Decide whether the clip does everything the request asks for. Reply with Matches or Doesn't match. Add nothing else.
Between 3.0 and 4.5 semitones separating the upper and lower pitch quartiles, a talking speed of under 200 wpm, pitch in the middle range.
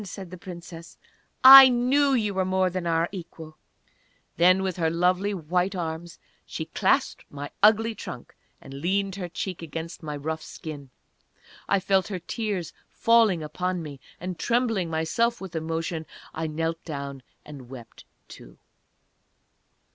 Matches